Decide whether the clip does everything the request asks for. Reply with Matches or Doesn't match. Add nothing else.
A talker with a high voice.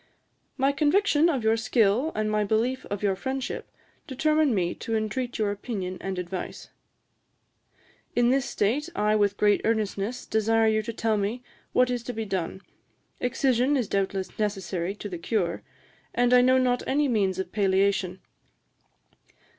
Matches